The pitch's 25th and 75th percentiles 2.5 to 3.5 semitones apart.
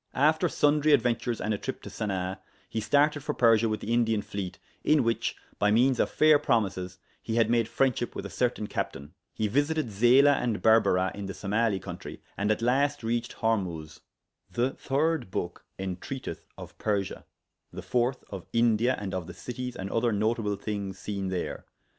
No: average, 4.1 semitones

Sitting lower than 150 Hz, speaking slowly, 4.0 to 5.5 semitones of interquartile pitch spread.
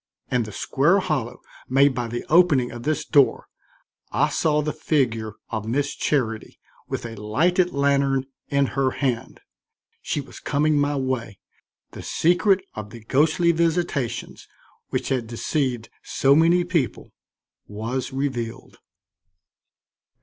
Yes: low, 135 Hz; slow, 130 wpm; average, 4.4 semitones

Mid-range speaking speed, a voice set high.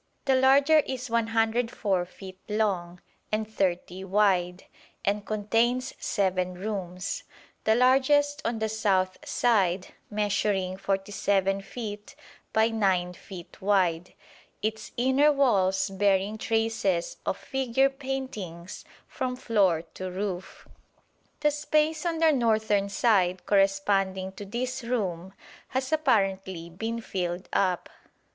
No: slow, 110 wpm; high, 205 Hz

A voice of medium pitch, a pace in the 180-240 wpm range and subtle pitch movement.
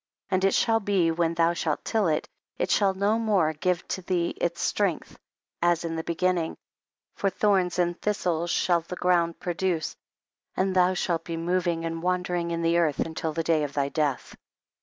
Yes: medium, 175 Hz; average, 185 wpm; narrow, 1.9 semitones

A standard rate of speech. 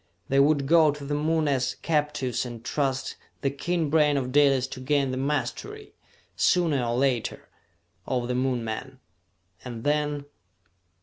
Yes: average, 150 wpm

